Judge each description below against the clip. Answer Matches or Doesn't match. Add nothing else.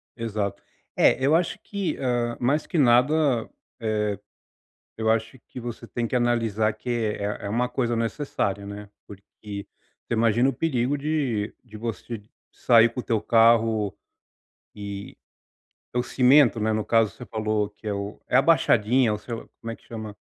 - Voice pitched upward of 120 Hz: Doesn't match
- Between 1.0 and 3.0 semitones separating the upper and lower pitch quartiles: Matches